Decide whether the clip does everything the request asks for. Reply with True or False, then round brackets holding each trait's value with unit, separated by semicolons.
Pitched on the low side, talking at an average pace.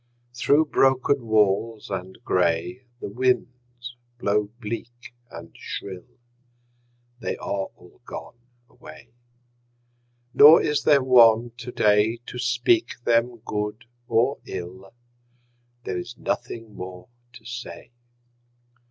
False (115 Hz; 105 wpm)